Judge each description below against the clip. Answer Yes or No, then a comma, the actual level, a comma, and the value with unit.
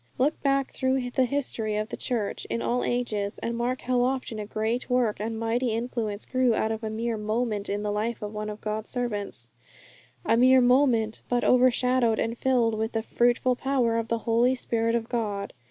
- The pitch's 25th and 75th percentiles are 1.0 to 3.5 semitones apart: Yes, narrow, 2.4 semitones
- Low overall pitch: No, high, 230 Hz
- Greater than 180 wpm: Yes, average, 195 wpm